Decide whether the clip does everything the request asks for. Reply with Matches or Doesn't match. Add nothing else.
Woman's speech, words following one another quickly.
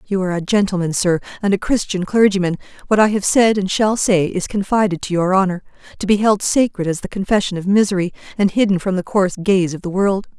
Matches